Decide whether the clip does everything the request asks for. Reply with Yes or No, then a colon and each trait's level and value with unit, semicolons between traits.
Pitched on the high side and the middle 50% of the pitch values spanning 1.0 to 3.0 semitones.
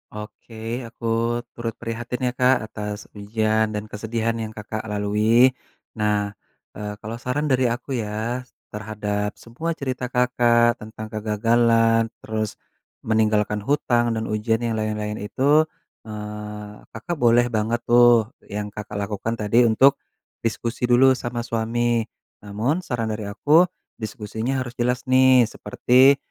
No: low, 115 Hz; narrow, 2.4 semitones